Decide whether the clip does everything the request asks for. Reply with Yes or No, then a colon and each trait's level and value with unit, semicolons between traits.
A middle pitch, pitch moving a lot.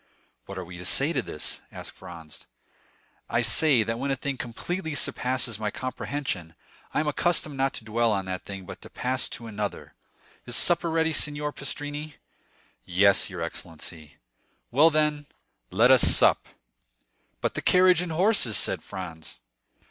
No: low, 125 Hz; wide, 7.5 semitones